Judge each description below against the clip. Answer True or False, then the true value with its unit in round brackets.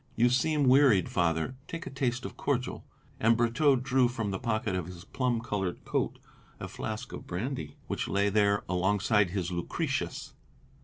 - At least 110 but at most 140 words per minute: False (165 wpm)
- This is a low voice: True (110 Hz)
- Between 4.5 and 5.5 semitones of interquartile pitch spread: True (5.1 semitones)